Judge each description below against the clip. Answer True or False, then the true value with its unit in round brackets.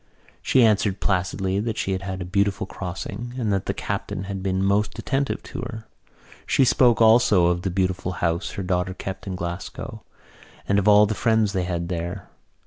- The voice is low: True (95 Hz)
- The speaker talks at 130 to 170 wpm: False (190 wpm)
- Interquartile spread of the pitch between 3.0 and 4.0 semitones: False (2.6 semitones)